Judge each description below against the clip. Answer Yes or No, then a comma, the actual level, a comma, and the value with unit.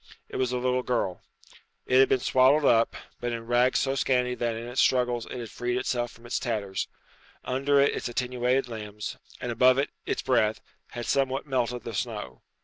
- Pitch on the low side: Yes, low, 125 Hz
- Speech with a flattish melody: Yes, narrow, 1.7 semitones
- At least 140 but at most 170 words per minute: No, average, 195 wpm